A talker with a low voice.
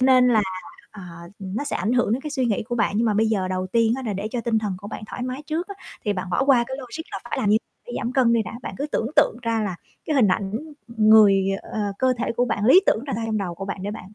No: high, 225 Hz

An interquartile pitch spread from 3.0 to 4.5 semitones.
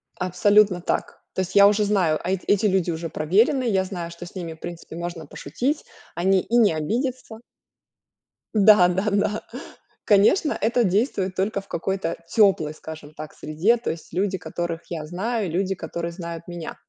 Yes: average, 3.6 semitones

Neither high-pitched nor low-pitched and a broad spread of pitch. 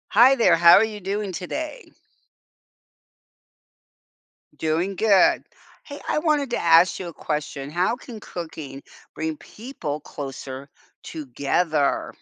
Yes: medium, 175 Hz; wide, 6.4 semitones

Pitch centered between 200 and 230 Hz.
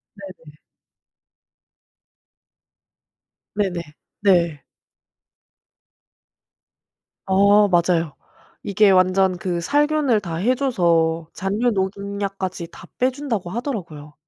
No: high, 190 Hz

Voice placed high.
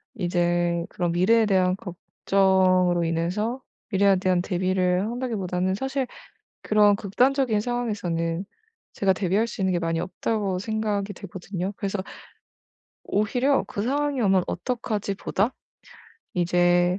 Yes: high, 195 Hz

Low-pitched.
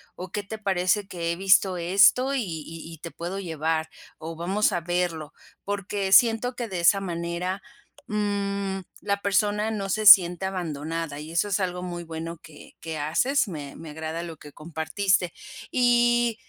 No: medium, 180 Hz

